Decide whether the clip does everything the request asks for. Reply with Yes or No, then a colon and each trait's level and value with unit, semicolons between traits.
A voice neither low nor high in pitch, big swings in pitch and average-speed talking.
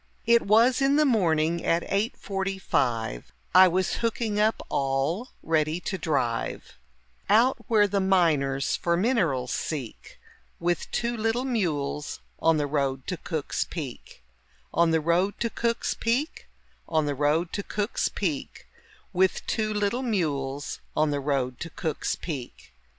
Yes: medium, 170 Hz; wide, 6.5 semitones; average, 145 wpm